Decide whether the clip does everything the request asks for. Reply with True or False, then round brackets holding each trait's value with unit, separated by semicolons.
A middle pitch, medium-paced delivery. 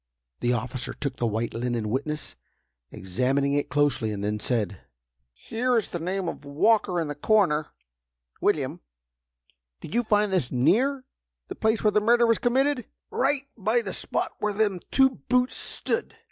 True (180 Hz; 160 wpm)